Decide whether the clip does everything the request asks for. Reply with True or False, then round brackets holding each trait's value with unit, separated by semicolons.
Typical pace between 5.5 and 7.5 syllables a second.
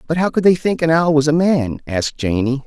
True (5.7 syllables/s)